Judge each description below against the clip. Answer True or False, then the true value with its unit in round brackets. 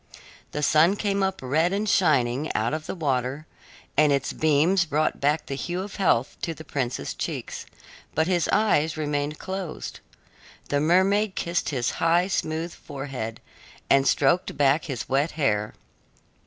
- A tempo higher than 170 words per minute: False (155 wpm)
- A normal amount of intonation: True (4.2 semitones)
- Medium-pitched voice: True (155 Hz)